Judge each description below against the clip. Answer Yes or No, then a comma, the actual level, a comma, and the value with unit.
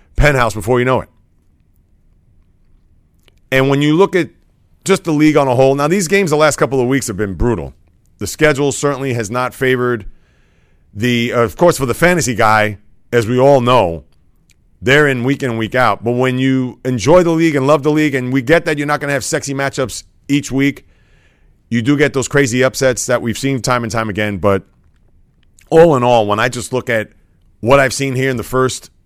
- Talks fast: Yes, fast, 215 wpm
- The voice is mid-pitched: No, low, 125 Hz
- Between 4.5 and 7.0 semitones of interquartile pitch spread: Yes, average, 4.8 semitones